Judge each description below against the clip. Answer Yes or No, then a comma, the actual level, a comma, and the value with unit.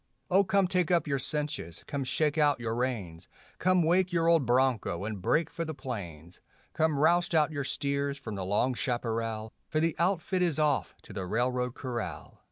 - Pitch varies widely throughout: Yes, wide, 6.2 semitones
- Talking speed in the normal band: Yes, average, 185 wpm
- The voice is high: No, medium, 140 Hz